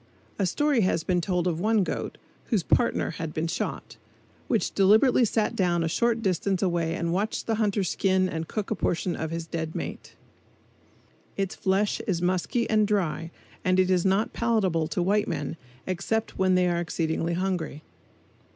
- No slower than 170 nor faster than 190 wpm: Yes, average, 175 wpm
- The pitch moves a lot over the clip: No, average, 3.6 semitones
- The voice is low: No, medium, 185 Hz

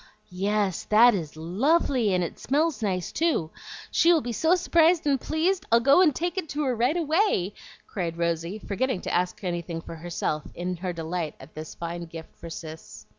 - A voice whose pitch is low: No, high, 200 Hz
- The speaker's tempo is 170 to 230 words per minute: Yes, average, 190 wpm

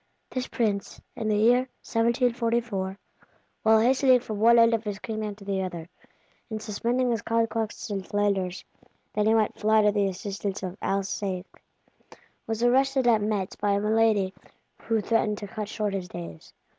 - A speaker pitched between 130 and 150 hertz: No, high, 215 Hz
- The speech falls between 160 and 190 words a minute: Yes, average, 165 wpm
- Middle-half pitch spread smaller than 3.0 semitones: Yes, narrow, 2.4 semitones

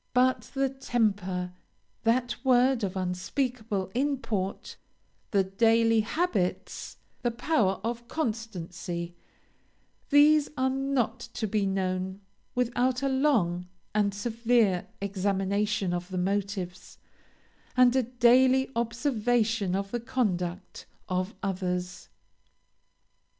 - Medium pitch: No, high, 220 Hz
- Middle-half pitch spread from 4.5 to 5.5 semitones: Yes, average, 4.9 semitones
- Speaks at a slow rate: Yes, slow, 100 wpm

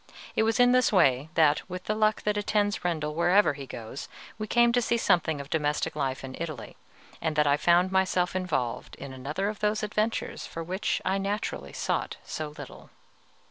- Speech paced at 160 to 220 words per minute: Yes, average, 190 wpm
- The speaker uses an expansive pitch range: Yes, wide, 5.9 semitones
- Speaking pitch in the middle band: Yes, medium, 180 Hz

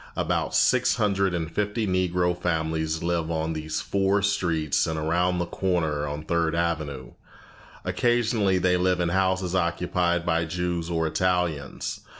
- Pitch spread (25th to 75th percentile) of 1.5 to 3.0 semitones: Yes, narrow, 2.4 semitones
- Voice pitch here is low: Yes, very low, 85 Hz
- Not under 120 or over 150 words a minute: Yes, average, 145 wpm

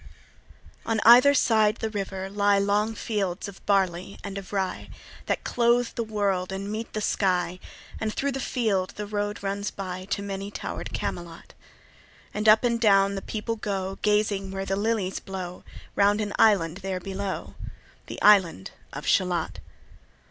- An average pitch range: No, narrow, 1.9 semitones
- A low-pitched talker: No, high, 200 Hz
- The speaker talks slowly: No, average, 160 wpm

